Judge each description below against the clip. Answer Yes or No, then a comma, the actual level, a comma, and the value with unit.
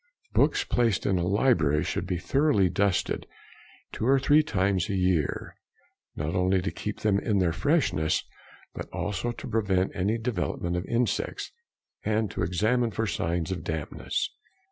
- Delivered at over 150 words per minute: Yes, average, 160 wpm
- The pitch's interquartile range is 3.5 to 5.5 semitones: Yes, average, 4.2 semitones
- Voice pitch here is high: No, very low, 95 Hz